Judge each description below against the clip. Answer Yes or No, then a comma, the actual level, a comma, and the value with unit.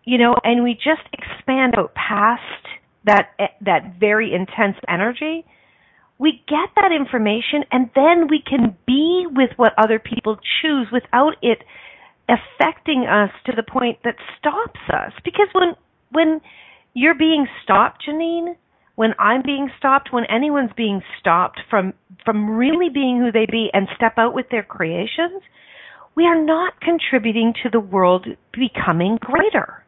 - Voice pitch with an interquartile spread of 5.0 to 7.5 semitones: Yes, wide, 5.6 semitones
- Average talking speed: Yes, average, 150 wpm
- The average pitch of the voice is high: Yes, very high, 250 Hz